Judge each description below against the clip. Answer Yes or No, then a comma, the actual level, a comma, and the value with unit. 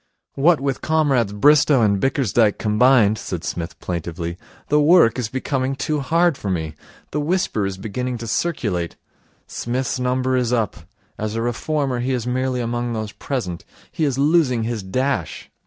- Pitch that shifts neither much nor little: Yes, average, 4.3 semitones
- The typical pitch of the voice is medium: No, low, 125 Hz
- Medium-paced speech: Yes, average, 160 wpm